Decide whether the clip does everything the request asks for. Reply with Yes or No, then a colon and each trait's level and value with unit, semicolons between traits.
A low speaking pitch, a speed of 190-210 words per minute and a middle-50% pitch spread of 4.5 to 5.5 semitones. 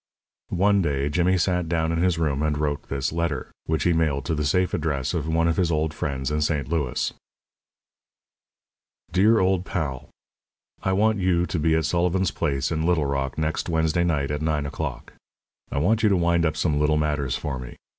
No: very low, 80 Hz; average, 195 wpm; average, 3.0 semitones